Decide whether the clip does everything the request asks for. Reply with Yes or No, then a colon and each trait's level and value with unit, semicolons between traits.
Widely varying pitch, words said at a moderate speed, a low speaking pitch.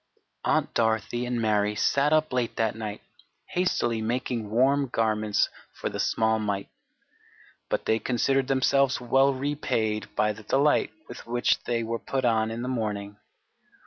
No: average, 3.3 semitones; average, 150 wpm; low, 115 Hz